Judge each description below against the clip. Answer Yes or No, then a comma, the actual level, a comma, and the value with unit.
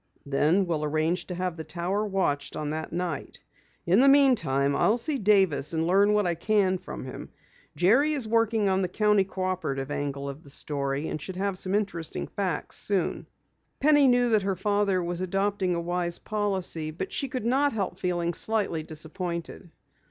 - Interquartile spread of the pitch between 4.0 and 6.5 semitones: Yes, average, 4.4 semitones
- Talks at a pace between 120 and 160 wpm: No, average, 180 wpm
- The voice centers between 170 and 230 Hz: Yes, medium, 185 Hz